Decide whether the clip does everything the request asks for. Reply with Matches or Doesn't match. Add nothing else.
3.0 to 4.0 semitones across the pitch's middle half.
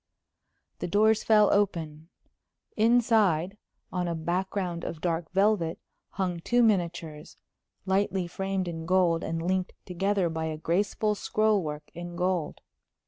Matches